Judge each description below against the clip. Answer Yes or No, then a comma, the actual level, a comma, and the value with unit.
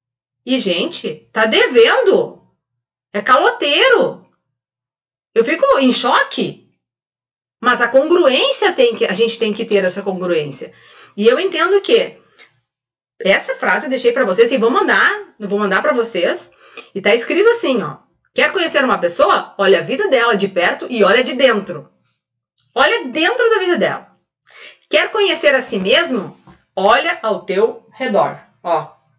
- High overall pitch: Yes, very high, 260 Hz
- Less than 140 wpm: No, average, 150 wpm